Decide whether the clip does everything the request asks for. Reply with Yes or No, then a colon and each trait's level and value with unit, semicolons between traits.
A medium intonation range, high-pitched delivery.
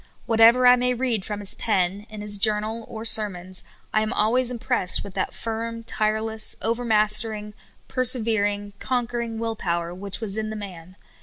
No: narrow, 2.0 semitones; high, 215 Hz